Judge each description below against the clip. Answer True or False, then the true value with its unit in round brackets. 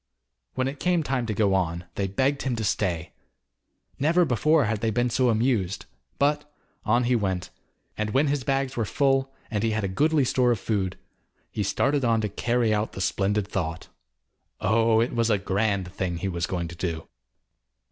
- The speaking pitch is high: False (110 Hz)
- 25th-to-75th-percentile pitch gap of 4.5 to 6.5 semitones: True (5.3 semitones)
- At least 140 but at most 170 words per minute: False (190 wpm)